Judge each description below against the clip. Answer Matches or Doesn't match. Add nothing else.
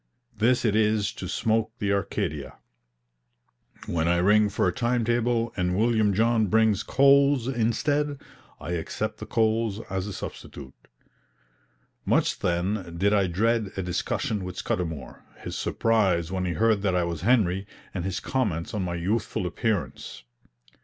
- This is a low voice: Matches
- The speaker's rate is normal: Matches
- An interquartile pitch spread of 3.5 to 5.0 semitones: Matches